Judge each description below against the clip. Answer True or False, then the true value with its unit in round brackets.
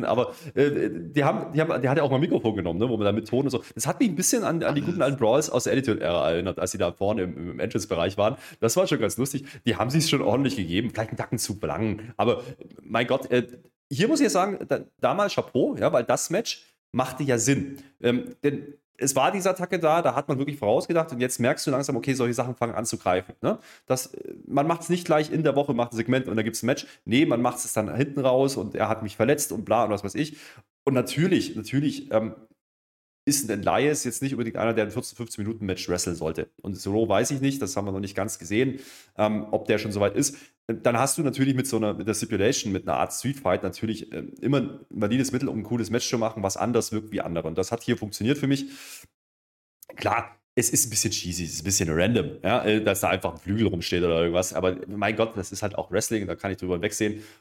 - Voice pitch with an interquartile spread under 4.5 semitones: False (4.9 semitones)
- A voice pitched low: True (115 Hz)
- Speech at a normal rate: False (260 wpm)